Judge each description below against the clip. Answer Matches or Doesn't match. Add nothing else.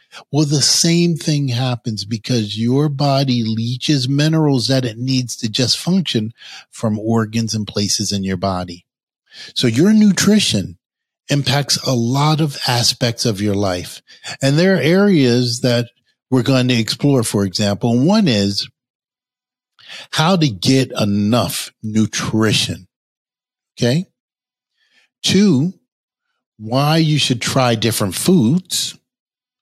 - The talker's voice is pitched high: Doesn't match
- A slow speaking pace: Matches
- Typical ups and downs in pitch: Matches